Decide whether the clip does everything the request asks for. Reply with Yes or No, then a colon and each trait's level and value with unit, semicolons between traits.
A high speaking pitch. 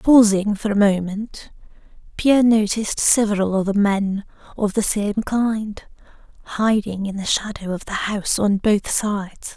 Yes: high, 205 Hz